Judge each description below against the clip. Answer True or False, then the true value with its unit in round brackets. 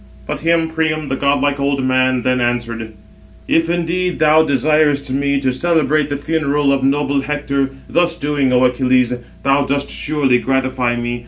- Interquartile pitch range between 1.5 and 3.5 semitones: True (2.9 semitones)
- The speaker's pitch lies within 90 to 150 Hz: True (140 Hz)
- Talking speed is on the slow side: False (160 wpm)